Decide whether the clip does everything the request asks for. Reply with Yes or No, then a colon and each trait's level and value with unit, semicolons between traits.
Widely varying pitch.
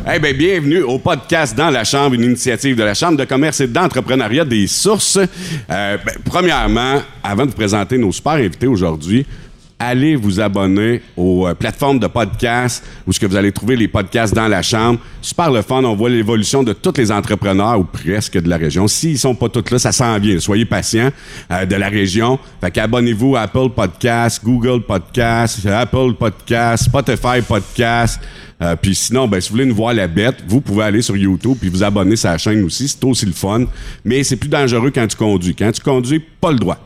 No: average, 4.2 semitones